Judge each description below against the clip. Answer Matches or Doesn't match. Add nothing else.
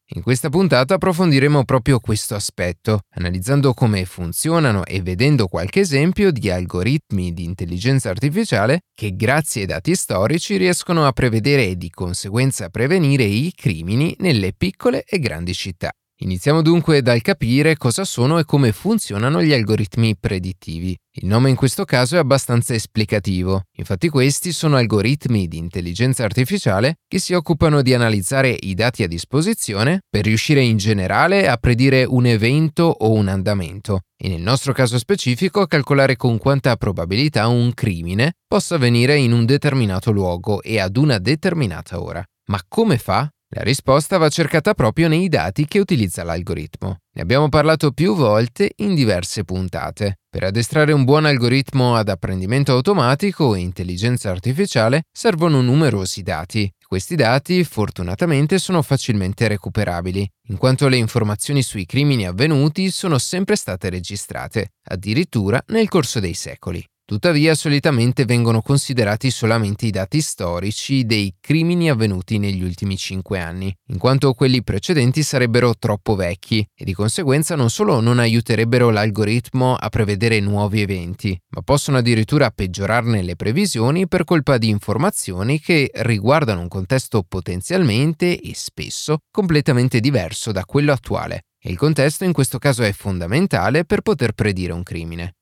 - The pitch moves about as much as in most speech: Doesn't match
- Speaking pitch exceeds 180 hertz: Doesn't match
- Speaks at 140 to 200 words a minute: Matches